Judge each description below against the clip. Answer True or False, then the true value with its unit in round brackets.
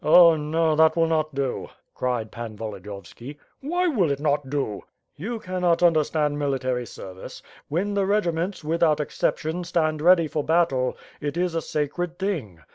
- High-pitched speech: False (155 Hz)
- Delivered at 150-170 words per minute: True (160 wpm)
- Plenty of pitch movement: False (4.0 semitones)